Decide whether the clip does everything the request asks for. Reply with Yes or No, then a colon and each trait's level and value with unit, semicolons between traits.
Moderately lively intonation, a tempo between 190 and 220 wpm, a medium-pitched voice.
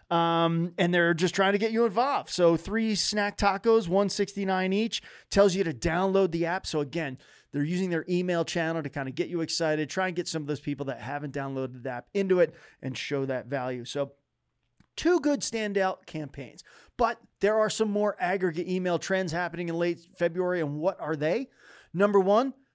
Yes: average, 4.1 semitones; average, 200 wpm; medium, 175 Hz